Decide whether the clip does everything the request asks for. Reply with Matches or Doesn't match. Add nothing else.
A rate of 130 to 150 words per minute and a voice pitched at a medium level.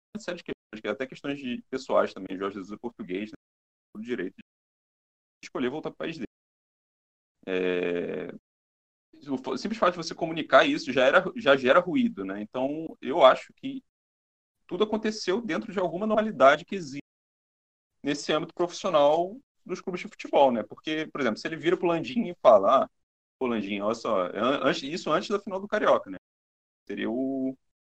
Doesn't match